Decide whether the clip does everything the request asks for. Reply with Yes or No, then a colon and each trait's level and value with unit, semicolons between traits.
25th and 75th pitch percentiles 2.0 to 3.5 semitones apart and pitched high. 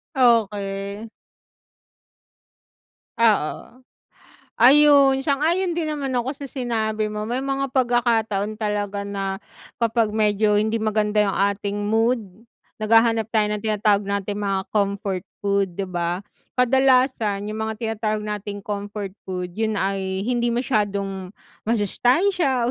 Yes: average, 3.2 semitones; high, 215 Hz